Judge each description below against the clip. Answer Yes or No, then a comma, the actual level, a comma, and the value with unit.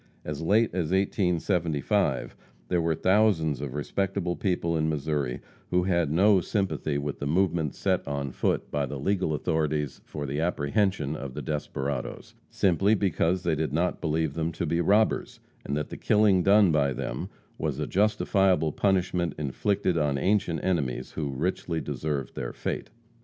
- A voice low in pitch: Yes, very low, 80 Hz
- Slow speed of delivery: No, average, 160 wpm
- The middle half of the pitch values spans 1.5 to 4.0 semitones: No, average, 4.4 semitones